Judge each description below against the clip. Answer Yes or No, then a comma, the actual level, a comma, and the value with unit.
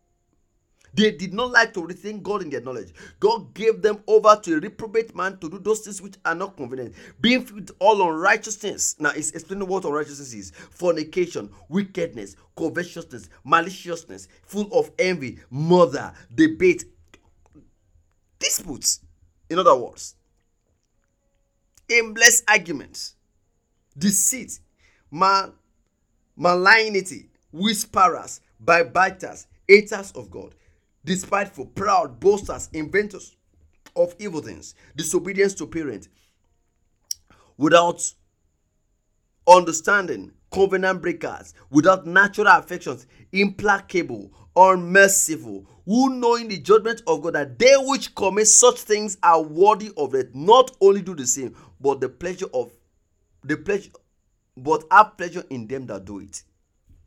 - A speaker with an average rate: No, slow, 120 wpm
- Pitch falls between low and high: Yes, medium, 175 Hz